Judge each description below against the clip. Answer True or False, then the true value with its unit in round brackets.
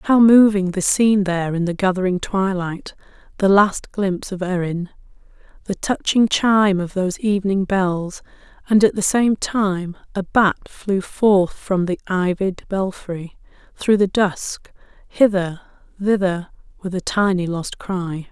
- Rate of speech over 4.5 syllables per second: False (4.2 syllables/s)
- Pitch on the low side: False (190 Hz)